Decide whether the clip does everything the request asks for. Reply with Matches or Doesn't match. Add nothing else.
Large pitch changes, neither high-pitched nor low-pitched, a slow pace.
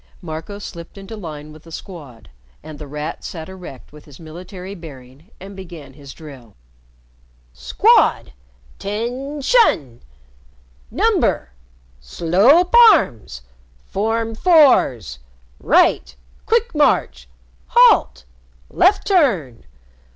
Matches